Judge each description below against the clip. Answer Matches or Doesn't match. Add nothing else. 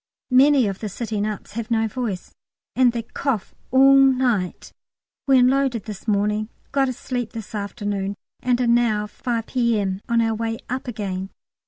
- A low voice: Doesn't match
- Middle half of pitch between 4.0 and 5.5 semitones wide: Doesn't match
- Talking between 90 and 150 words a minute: Doesn't match